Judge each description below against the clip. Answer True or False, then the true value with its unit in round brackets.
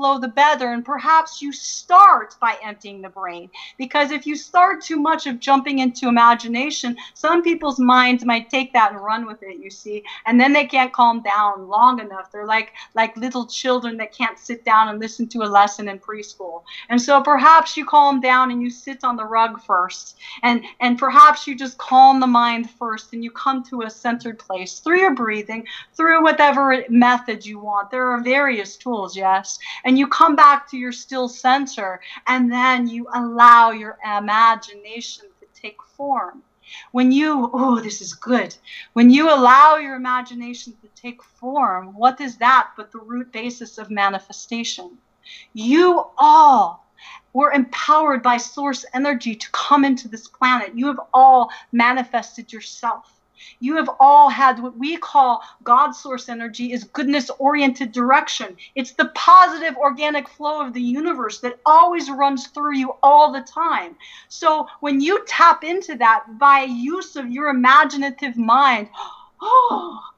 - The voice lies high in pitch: True (255 Hz)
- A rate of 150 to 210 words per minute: True (170 wpm)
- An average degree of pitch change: True (3.8 semitones)